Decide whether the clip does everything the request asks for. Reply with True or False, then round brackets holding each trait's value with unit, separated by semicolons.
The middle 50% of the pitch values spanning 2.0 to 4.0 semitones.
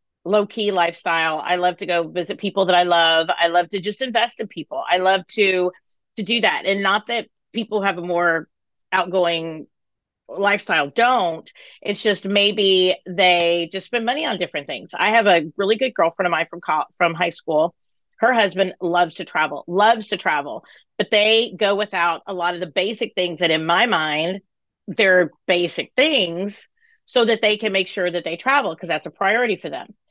True (3.5 semitones)